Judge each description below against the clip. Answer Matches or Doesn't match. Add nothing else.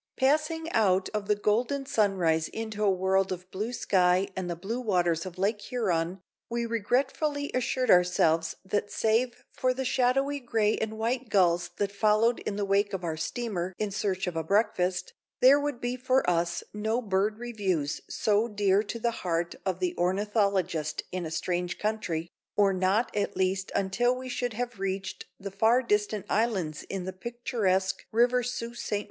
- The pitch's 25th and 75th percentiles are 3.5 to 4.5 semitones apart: Matches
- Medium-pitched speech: Doesn't match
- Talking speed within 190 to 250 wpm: Doesn't match